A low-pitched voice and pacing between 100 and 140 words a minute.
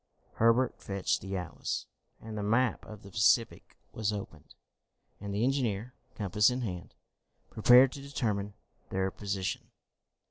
Yes: low, 105 Hz; slow, 135 wpm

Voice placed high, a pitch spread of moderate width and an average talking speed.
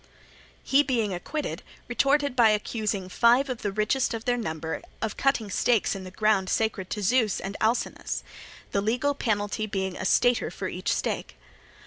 Yes: high, 220 Hz; average, 3.8 semitones; average, 165 wpm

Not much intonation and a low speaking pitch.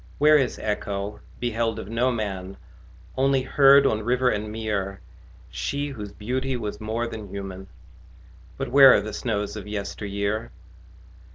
No: average, 3.8 semitones; low, 110 Hz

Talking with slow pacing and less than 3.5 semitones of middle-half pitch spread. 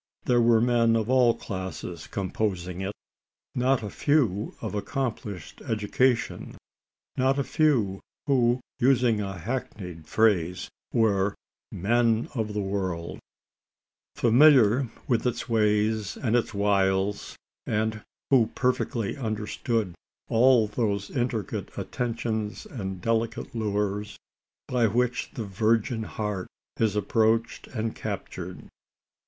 Yes: slow, 110 wpm; average, 3.0 semitones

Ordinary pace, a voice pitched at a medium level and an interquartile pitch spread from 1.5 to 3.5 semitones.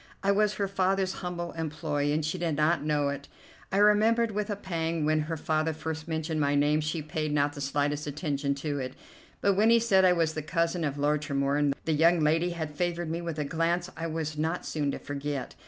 No: fast, 220 wpm; medium, 160 Hz; average, 2.9 semitones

